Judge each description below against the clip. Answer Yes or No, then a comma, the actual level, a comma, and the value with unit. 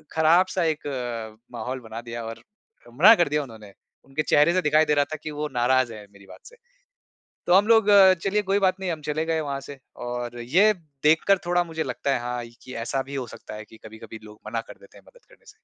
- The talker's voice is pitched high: No, medium, 145 Hz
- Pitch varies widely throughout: Yes, wide, 6.4 semitones